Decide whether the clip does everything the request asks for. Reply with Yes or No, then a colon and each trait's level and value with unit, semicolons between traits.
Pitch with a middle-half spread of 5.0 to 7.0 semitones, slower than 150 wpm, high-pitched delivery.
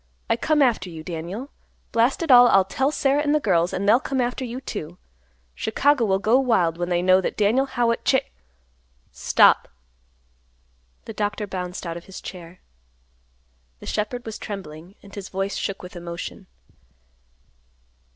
No: wide, 5.4 semitones; average, 160 wpm; high, 205 Hz